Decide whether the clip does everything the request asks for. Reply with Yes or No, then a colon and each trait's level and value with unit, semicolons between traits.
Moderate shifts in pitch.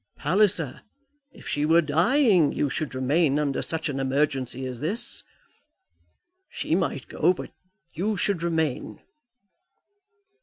Yes: average, 4.1 semitones